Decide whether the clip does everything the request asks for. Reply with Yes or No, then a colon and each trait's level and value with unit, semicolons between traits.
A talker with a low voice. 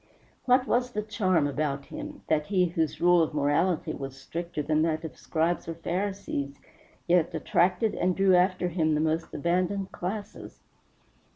No: medium, 175 Hz